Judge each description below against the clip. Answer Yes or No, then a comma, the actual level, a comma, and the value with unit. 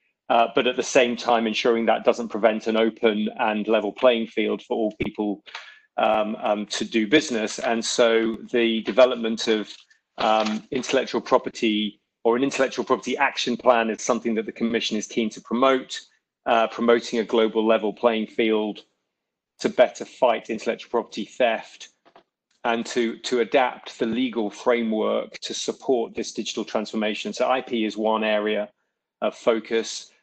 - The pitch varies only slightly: Yes, narrow, 1.6 semitones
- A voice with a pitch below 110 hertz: No, low, 115 Hz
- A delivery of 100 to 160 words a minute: Yes, average, 155 wpm